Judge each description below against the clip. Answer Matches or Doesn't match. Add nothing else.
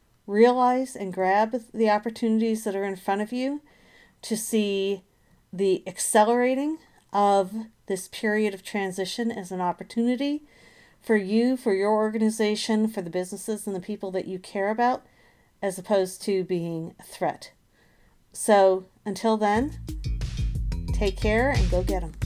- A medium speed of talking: Matches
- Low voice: Doesn't match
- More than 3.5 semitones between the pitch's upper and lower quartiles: Doesn't match